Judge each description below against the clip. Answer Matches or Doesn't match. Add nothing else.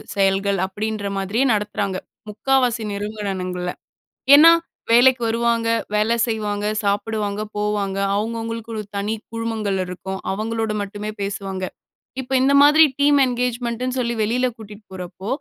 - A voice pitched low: Doesn't match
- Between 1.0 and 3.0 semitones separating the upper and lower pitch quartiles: Matches